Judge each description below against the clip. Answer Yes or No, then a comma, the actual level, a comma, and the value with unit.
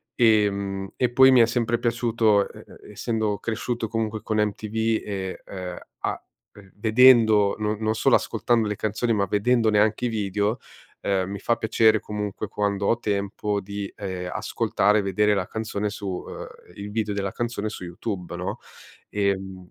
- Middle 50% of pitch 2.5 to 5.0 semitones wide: No, narrow, 2.1 semitones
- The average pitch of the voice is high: No, low, 105 Hz